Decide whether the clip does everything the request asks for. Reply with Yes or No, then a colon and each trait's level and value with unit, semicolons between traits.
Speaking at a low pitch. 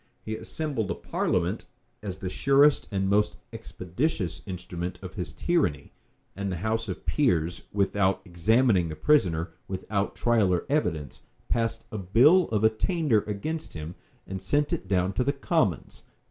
Yes: low, 100 Hz